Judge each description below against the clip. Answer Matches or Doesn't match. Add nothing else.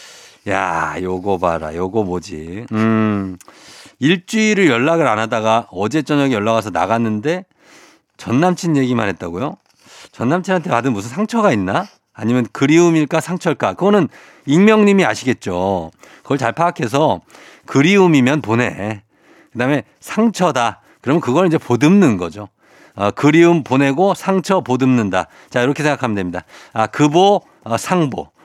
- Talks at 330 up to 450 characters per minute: Doesn't match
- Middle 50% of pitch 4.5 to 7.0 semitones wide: Doesn't match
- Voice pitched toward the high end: Doesn't match